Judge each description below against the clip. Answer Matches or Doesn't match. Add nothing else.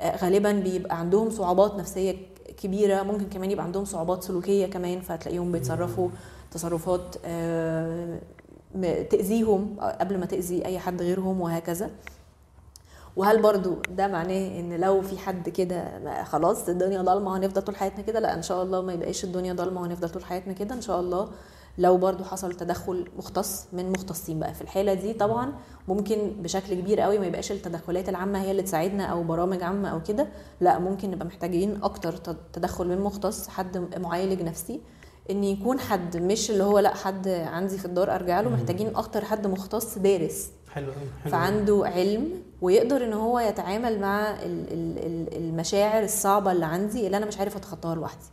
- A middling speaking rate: Doesn't match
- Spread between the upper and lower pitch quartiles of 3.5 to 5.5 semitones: Doesn't match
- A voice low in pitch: Doesn't match